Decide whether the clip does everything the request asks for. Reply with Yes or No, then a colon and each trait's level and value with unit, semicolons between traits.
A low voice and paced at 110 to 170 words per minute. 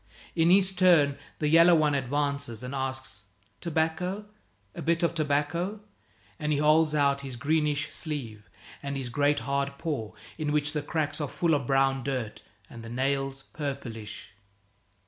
No: medium, 145 Hz; average, 155 wpm